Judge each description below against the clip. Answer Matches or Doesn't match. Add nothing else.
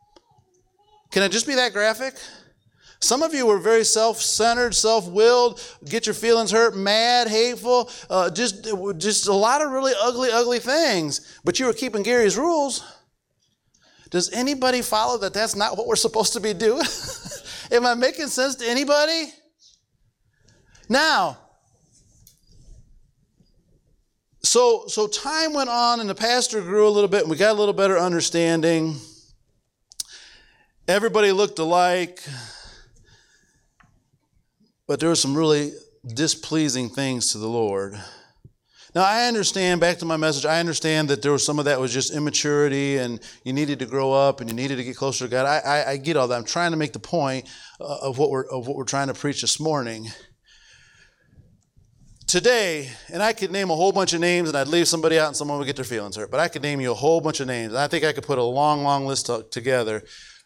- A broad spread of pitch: Matches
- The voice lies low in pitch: Doesn't match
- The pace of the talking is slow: Doesn't match